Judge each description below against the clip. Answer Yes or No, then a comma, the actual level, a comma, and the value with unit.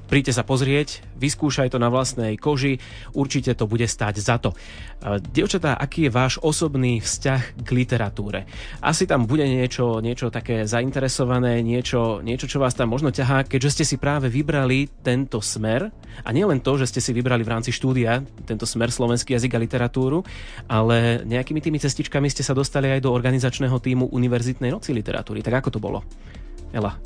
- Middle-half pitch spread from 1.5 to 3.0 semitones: Yes, average, 2.7 semitones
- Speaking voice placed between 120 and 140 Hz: Yes, low, 125 Hz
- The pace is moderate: No, fast, 175 wpm